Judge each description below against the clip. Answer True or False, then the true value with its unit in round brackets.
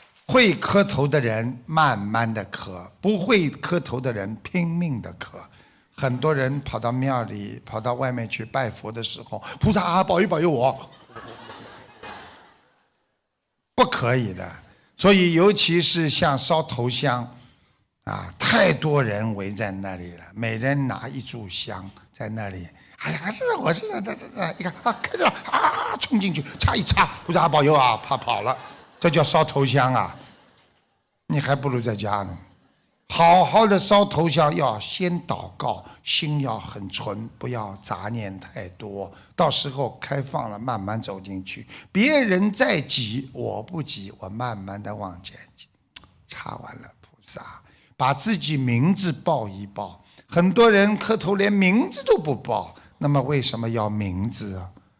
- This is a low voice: True (130 Hz)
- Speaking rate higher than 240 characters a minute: False (210 characters per minute)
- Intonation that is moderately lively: False (7.7 semitones)